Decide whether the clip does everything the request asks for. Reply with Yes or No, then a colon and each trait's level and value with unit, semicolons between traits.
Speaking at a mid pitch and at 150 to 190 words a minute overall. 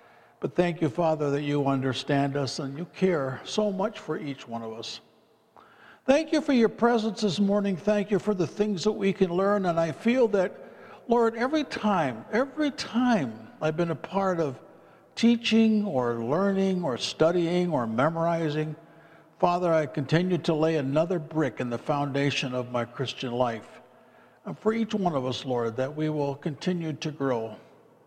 Yes: medium, 165 Hz; average, 175 wpm